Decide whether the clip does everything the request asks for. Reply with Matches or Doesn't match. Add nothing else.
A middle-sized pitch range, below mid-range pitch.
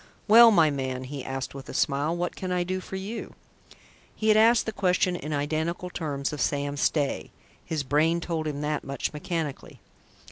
Doesn't match